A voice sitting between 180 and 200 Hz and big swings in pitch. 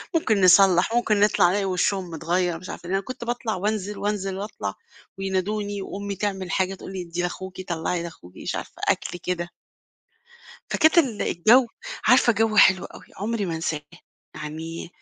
No: high, 190 Hz; average, 2.9 semitones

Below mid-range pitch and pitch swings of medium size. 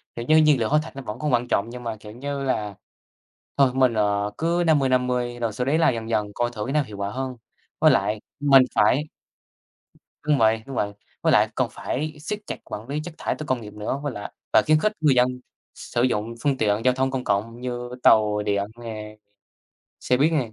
Yes: low, 125 Hz; average, 4.4 semitones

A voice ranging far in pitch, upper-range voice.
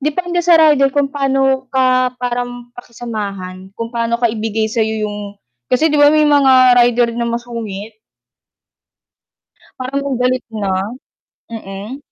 No: average, 3.5 semitones; high, 245 Hz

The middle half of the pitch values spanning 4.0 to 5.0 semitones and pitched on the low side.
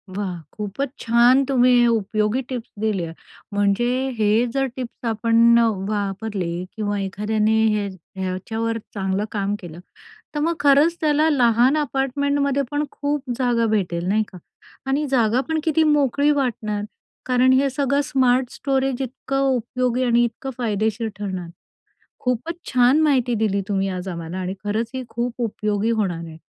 No: average, 4.6 semitones; high, 235 Hz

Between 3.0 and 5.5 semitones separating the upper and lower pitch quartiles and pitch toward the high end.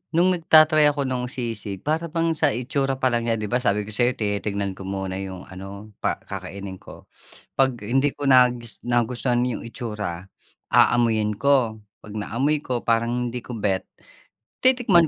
No: average, 4.6 semitones; low, 120 Hz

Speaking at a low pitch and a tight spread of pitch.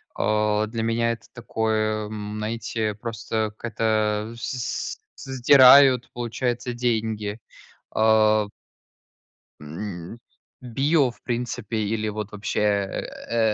Yes: low, 110 Hz; narrow, 1.9 semitones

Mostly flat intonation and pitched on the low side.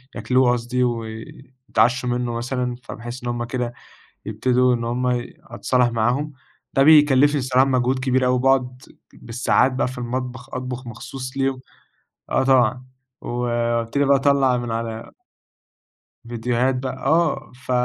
Yes: narrow, 1.5 semitones; low, 125 Hz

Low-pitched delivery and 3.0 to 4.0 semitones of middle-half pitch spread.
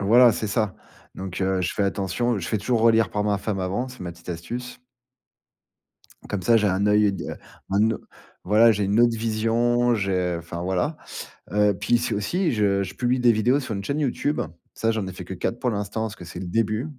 Yes: low, 105 Hz; average, 3.6 semitones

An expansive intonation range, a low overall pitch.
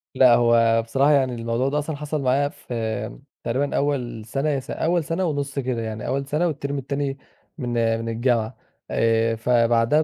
No: average, 3.7 semitones; low, 130 Hz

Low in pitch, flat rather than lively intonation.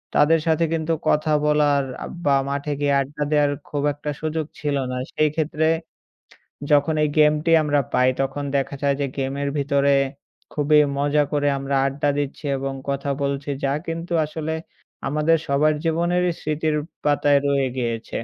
No: medium, 145 Hz; narrow, 1.6 semitones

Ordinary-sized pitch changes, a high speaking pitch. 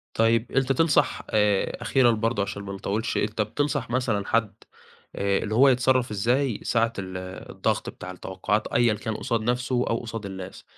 No: average, 3.3 semitones; low, 115 Hz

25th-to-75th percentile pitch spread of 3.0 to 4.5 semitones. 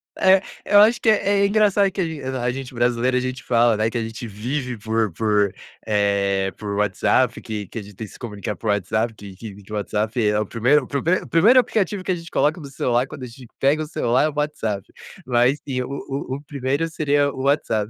No: wide, 5.5 semitones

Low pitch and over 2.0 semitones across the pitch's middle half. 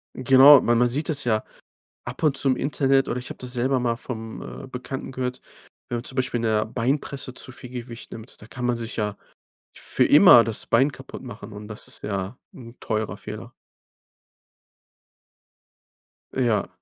Yes: low, 125 Hz; narrow, 2.5 semitones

